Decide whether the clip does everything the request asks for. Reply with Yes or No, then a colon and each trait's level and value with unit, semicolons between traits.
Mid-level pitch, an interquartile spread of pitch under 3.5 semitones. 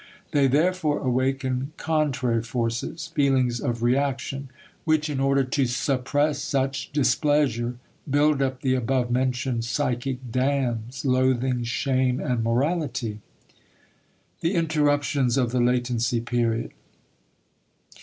No: low, 130 Hz; average, 2.7 semitones